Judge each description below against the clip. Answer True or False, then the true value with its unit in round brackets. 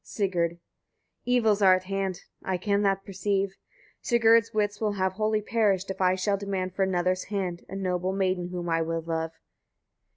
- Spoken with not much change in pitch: True (1.9 semitones)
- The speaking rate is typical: True (175 wpm)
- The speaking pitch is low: False (190 Hz)